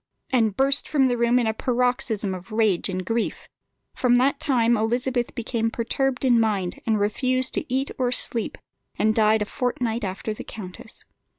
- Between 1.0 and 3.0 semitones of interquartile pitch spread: Yes, narrow, 2.6 semitones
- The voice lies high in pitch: Yes, high, 235 Hz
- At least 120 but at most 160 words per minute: No, average, 170 wpm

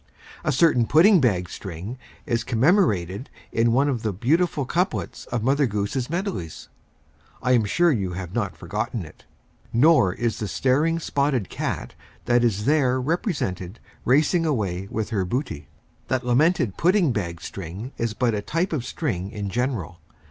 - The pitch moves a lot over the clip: Yes, wide, 6.7 semitones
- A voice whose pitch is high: No, low, 120 Hz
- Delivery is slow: No, average, 155 wpm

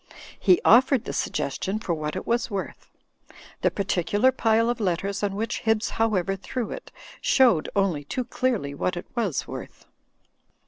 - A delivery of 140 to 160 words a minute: Yes, average, 155 wpm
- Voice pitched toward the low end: No, high, 205 Hz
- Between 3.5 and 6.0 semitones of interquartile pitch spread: Yes, average, 4.3 semitones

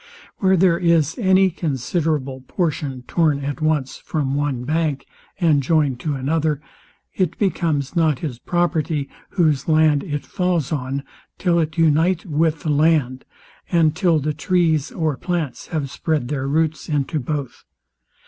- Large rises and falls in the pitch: No, average, 2.9 semitones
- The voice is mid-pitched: Yes, medium, 155 Hz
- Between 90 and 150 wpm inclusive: Yes, average, 145 wpm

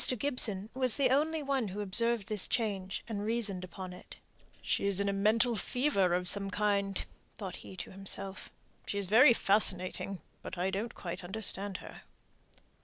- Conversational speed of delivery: Yes, average, 160 wpm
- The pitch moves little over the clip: No, average, 3.4 semitones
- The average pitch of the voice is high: Yes, high, 200 Hz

